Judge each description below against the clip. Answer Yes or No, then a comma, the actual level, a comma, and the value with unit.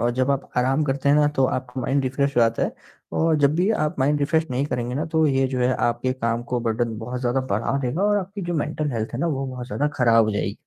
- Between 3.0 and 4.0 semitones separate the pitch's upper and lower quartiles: Yes, average, 3.3 semitones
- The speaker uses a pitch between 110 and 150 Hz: Yes, low, 135 Hz